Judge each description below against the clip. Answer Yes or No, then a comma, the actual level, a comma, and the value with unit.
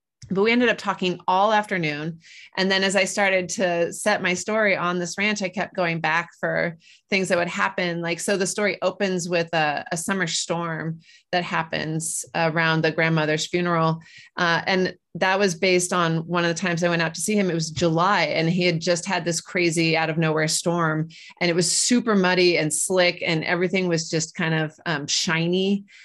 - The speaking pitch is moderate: Yes, medium, 175 Hz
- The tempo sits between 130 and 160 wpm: No, fast, 205 wpm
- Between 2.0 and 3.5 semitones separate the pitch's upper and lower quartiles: Yes, narrow, 2.4 semitones